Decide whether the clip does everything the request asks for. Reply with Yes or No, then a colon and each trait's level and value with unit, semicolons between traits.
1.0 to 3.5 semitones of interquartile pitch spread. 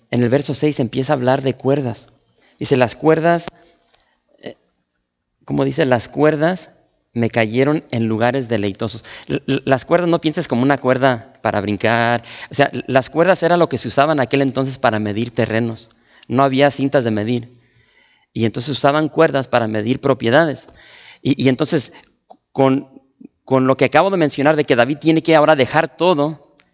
No: average, 4.2 semitones